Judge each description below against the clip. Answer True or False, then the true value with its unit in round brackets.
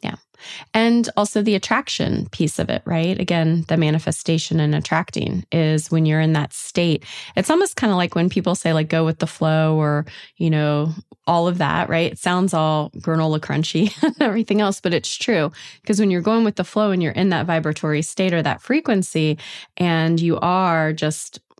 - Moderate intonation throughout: True (4.0 semitones)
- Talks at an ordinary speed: True (195 wpm)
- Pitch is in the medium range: True (165 Hz)